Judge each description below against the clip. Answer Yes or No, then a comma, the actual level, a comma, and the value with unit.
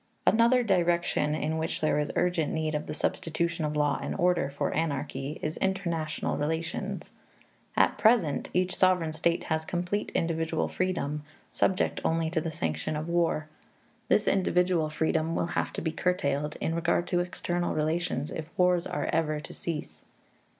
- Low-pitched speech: No, medium, 165 Hz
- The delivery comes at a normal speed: Yes, average, 160 wpm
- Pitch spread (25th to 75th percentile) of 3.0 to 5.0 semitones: No, narrow, 2.5 semitones